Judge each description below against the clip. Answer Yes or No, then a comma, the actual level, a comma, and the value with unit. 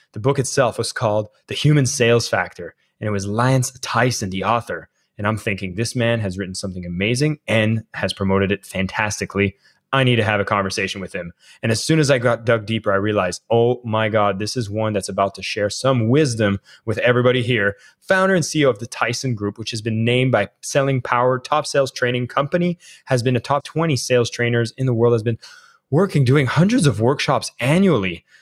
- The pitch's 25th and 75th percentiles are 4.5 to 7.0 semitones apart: No, average, 4.0 semitones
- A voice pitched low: Yes, low, 115 Hz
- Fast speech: Yes, fast, 210 wpm